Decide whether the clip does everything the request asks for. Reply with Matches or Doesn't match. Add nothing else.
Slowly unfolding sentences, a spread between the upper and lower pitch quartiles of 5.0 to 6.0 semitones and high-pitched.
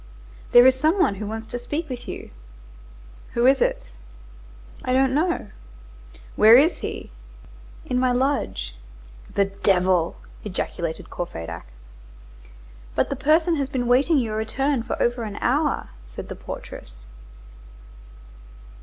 Matches